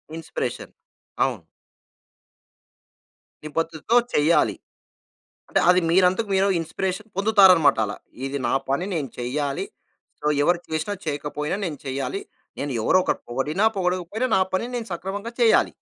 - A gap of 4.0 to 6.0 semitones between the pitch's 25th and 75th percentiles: Yes, average, 4.7 semitones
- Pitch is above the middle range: No, medium, 170 Hz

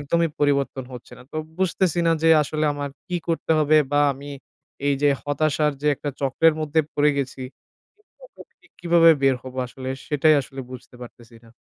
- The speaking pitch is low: No, medium, 145 Hz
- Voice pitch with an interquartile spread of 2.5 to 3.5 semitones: Yes, average, 2.9 semitones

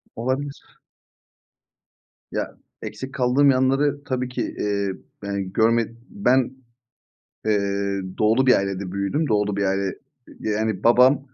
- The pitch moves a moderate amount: Yes, average, 4.8 semitones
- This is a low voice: Yes, low, 115 Hz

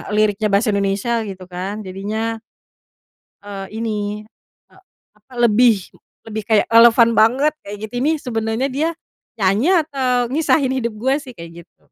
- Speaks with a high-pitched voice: Yes, high, 225 Hz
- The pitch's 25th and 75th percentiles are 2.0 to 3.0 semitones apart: No, average, 4.0 semitones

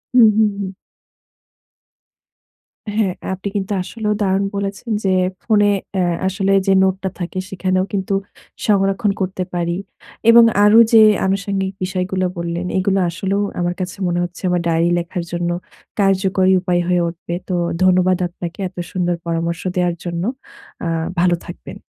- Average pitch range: No, narrow, 1.9 semitones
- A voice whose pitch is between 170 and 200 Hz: Yes, medium, 185 Hz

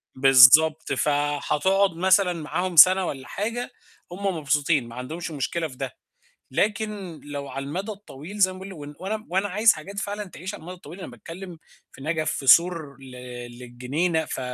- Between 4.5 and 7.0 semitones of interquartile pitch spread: Yes, average, 4.9 semitones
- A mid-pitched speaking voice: Yes, medium, 170 Hz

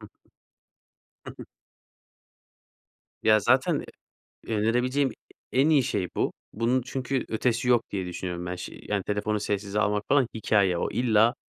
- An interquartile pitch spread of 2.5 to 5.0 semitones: Yes, average, 3.6 semitones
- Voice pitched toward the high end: No, low, 110 Hz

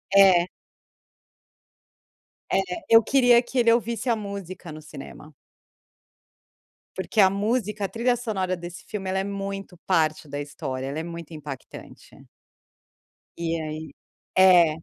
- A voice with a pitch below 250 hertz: Yes, high, 190 Hz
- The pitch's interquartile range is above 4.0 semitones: Yes, average, 4.8 semitones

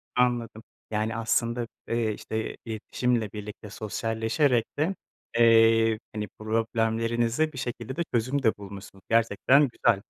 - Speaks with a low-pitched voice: Yes, low, 115 Hz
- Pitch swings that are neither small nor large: No, narrow, 1.6 semitones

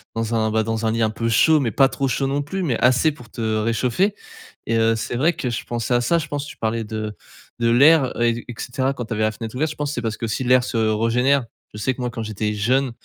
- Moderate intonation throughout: Yes, average, 3.2 semitones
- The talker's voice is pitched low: Yes, low, 120 Hz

